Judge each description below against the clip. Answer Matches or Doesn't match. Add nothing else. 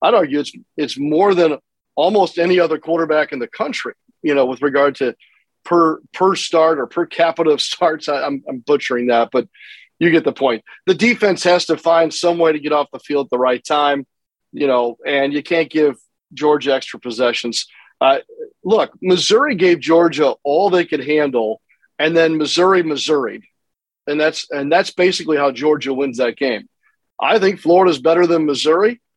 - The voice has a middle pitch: Matches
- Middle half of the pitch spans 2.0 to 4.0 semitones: Matches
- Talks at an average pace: Matches